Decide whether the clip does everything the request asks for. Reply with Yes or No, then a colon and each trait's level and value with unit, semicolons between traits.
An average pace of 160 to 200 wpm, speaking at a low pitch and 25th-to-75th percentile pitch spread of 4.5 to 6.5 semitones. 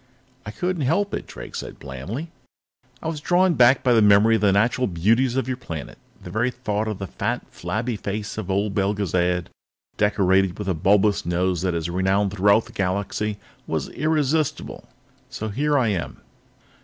Yes: average, 175 wpm; low, 105 Hz; average, 4.9 semitones